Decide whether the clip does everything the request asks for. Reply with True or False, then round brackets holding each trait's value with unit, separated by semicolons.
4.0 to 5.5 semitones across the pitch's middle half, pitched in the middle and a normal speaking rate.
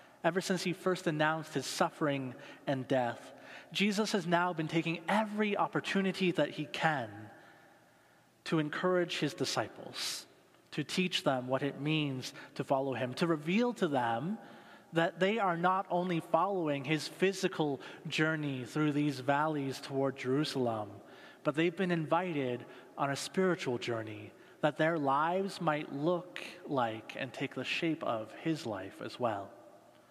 True (4.6 semitones; 155 Hz; 145 wpm)